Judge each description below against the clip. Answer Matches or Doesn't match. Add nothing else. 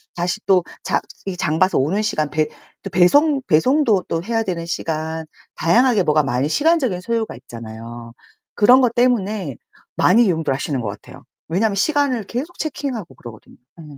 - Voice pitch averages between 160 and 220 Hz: Matches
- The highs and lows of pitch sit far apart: Matches